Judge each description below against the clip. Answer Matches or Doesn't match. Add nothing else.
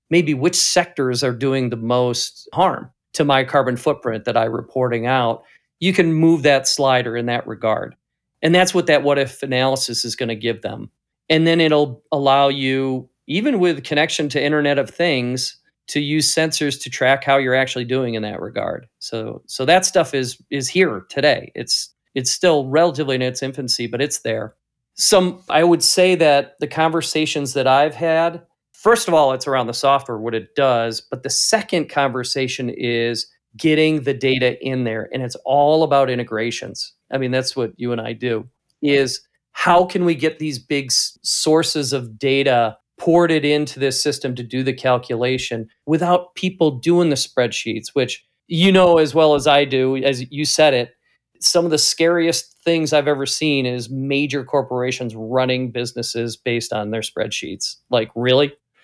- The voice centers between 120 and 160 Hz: Matches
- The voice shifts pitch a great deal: Doesn't match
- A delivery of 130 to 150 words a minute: Doesn't match